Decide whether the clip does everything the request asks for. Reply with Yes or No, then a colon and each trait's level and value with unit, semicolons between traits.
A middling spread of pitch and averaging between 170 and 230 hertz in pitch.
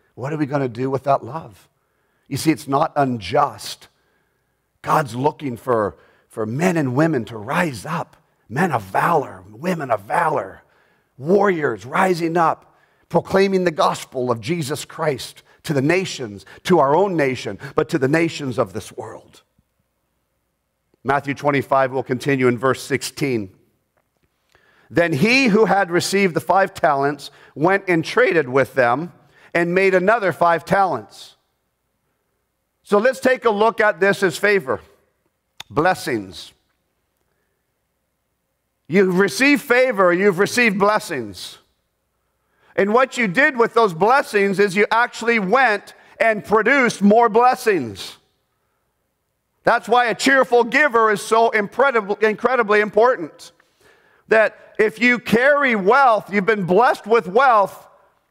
No: wide, 7.5 semitones; high, 190 Hz